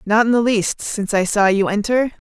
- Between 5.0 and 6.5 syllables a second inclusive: Yes, 5.2 syllables/s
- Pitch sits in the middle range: No, high, 215 Hz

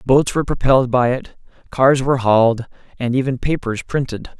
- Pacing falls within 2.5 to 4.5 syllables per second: No, 5.6 syllables/s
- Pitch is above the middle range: No, low, 130 Hz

